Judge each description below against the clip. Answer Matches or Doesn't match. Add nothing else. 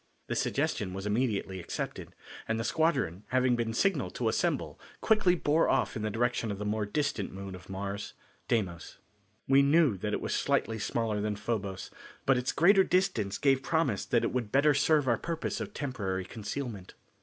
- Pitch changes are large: Matches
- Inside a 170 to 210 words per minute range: Matches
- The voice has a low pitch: Matches